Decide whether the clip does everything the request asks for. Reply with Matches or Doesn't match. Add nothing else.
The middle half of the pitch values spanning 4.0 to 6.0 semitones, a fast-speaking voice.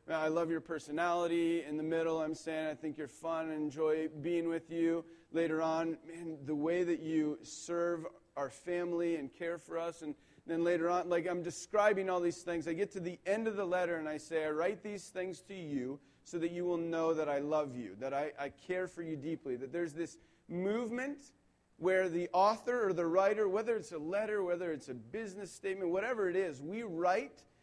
Doesn't match